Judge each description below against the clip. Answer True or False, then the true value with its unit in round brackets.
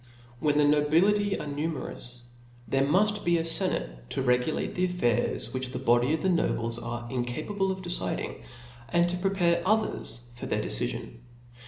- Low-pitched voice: False (150 Hz)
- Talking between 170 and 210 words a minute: False (155 wpm)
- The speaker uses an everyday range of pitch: False (6.6 semitones)